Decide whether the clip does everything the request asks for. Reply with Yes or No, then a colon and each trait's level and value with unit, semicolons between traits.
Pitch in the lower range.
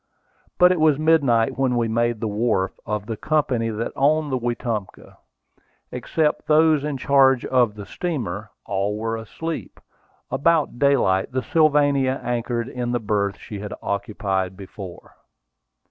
Yes: low, 120 Hz